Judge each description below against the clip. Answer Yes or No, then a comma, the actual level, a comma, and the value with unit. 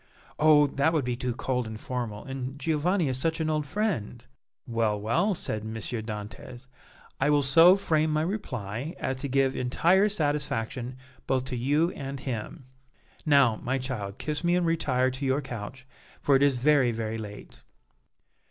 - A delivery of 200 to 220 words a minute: No, average, 170 wpm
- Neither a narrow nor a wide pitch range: Yes, average, 4.2 semitones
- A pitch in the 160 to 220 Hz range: No, low, 135 Hz